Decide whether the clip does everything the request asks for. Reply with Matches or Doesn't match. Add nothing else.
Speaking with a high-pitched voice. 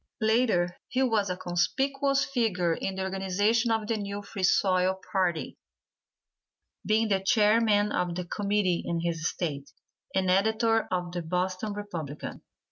Matches